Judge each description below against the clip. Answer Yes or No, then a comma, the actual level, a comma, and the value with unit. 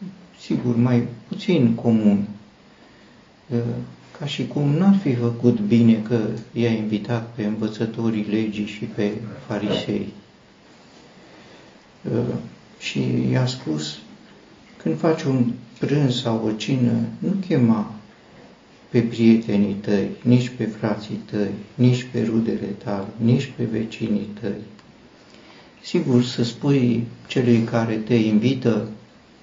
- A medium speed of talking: No, slow, 110 wpm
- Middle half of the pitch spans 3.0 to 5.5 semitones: No, narrow, 2.4 semitones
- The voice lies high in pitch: No, low, 115 Hz